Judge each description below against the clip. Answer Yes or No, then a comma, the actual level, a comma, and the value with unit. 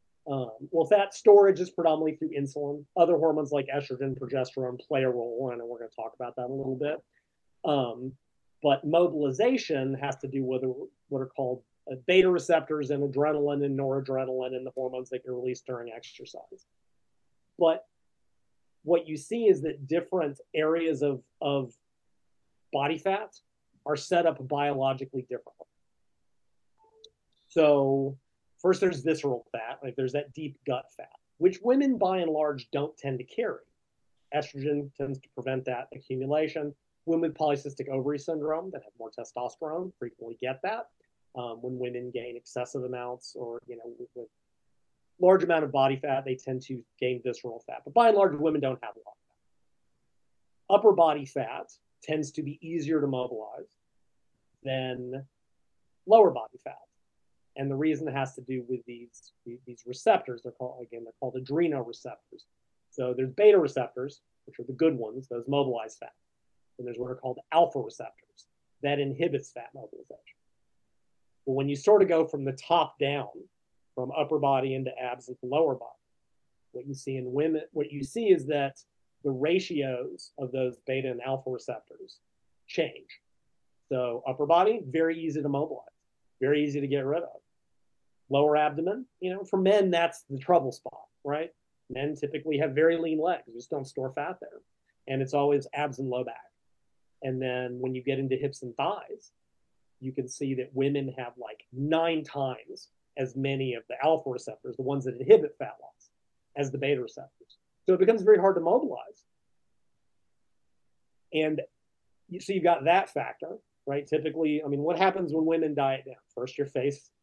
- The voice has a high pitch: No, medium, 140 Hz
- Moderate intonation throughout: Yes, average, 3.8 semitones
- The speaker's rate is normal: Yes, average, 170 wpm